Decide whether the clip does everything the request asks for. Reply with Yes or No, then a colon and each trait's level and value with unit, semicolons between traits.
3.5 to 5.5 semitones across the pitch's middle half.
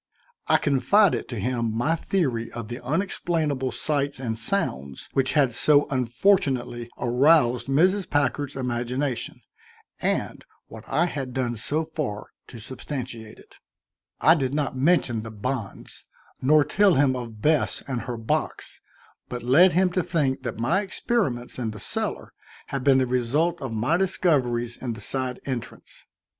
Yes: average, 4.4 semitones